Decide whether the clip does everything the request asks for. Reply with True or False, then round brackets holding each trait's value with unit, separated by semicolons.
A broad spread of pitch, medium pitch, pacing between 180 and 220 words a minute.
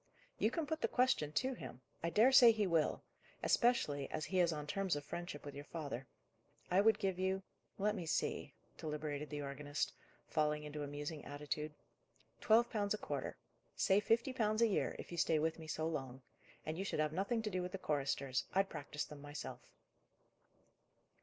True (5.7 semitones; 160 Hz; 190 wpm)